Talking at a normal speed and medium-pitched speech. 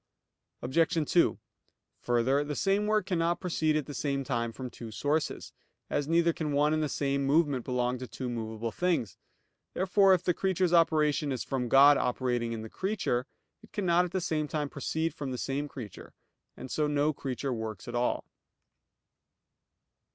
Yes: average, 170 wpm; medium, 145 Hz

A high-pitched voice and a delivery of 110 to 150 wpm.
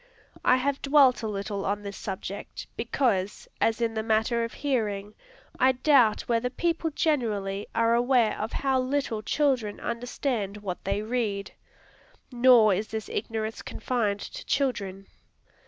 Yes: high, 225 Hz; average, 140 wpm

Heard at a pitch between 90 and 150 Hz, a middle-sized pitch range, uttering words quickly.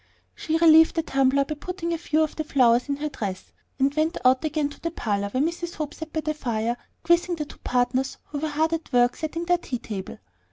No: very high, 300 Hz; average, 4.1 semitones; fast, 235 wpm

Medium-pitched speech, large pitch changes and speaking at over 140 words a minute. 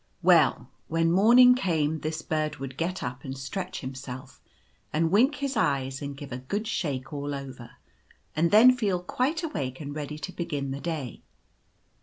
Yes: medium, 155 Hz; wide, 5.7 semitones; average, 170 wpm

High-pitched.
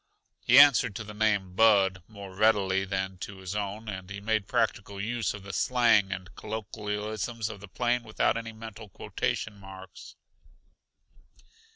No: low, 105 Hz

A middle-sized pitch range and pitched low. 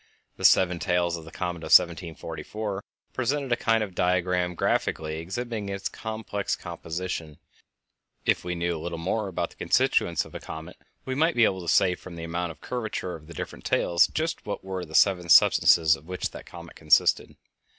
Yes: average, 3.5 semitones; very low, 90 Hz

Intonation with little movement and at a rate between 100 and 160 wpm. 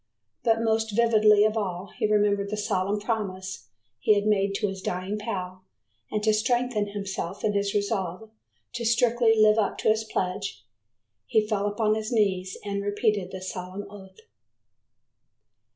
Yes: narrow, 2.1 semitones; average, 155 wpm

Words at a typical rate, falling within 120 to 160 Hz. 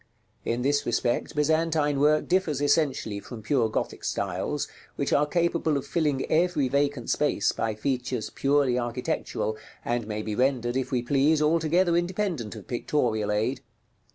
Yes: average, 150 wpm; medium, 140 Hz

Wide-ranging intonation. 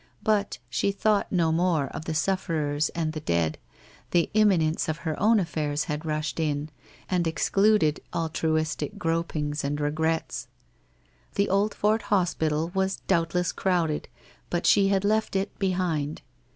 No: average, 3.9 semitones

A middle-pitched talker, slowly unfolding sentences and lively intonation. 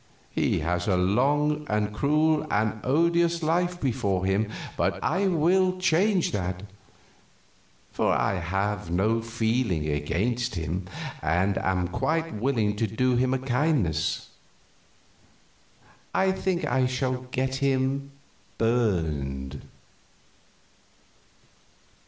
No: low, 120 Hz; slow, 105 wpm; wide, 7.9 semitones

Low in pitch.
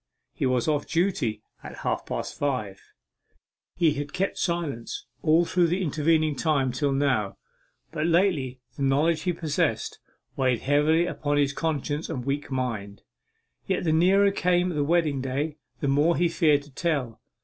No: medium, 145 Hz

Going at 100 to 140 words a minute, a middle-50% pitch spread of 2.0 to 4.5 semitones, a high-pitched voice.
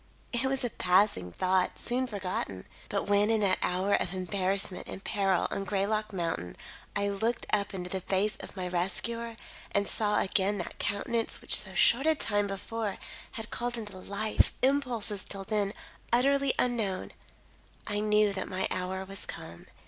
No: average, 165 wpm; average, 3.0 semitones; high, 200 Hz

